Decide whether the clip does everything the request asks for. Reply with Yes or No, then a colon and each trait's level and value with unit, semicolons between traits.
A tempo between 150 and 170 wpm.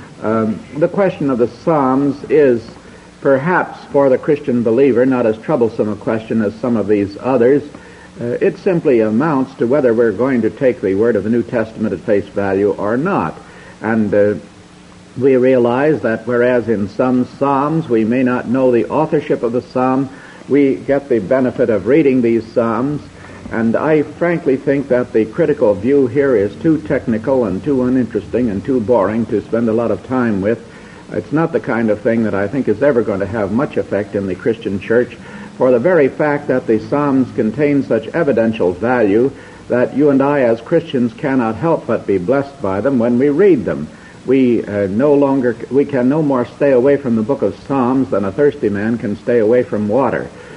No: average, 195 wpm